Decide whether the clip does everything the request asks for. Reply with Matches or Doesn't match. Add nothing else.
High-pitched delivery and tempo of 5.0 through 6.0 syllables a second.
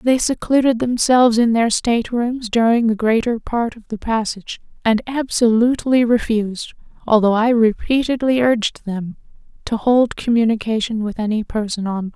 Matches